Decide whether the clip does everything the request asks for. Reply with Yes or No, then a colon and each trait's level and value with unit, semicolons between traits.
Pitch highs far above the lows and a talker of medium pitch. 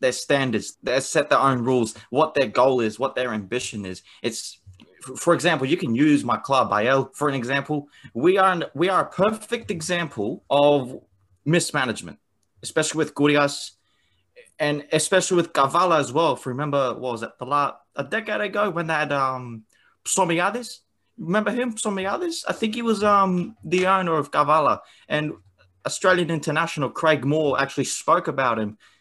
Yes: wide, 6.3 semitones; medium, 150 Hz